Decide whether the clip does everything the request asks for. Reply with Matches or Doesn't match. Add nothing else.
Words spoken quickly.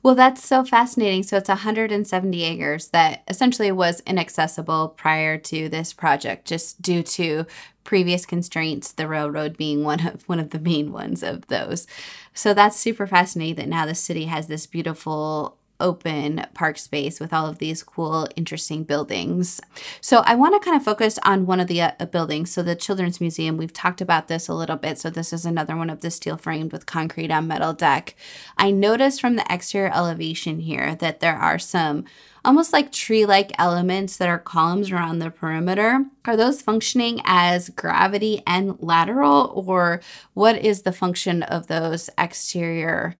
Doesn't match